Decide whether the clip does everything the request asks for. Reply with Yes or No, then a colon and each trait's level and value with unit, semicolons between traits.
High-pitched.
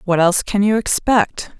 Yes: high, 200 Hz